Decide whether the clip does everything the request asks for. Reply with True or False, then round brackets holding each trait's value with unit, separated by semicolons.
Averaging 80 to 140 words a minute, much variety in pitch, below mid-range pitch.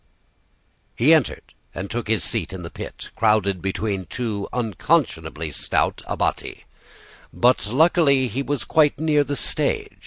True (135 wpm; 6.5 semitones; 115 Hz)